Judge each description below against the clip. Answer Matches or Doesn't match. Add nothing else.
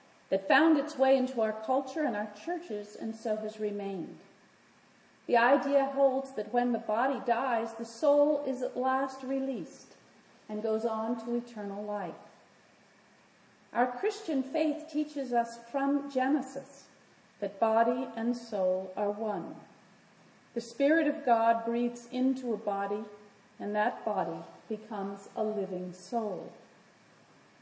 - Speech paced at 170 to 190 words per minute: Doesn't match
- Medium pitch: Doesn't match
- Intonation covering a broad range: Doesn't match